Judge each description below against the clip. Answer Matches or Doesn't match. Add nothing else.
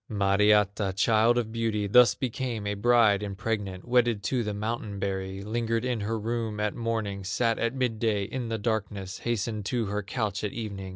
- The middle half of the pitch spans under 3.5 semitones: Matches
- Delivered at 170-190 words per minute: Matches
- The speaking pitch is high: Doesn't match